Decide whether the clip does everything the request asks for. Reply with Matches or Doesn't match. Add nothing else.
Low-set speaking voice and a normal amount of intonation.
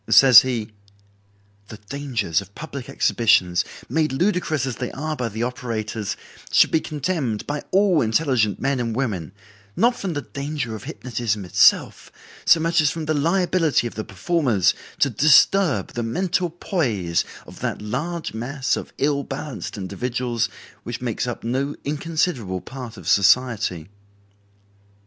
Doesn't match